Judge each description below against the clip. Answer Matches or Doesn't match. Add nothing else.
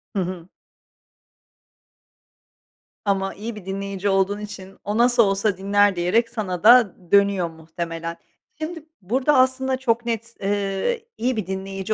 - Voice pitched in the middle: Doesn't match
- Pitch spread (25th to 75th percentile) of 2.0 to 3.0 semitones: Doesn't match